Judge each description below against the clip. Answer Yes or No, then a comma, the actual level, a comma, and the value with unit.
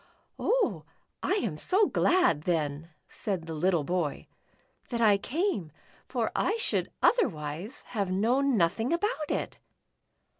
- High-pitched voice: Yes, high, 200 Hz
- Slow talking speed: Yes, slow, 125 wpm